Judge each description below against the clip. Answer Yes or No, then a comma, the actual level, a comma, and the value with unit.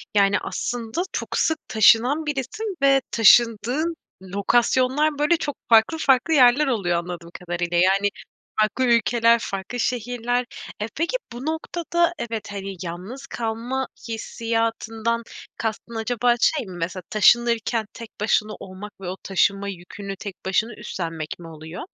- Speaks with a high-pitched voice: Yes, high, 225 Hz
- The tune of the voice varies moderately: Yes, average, 4.3 semitones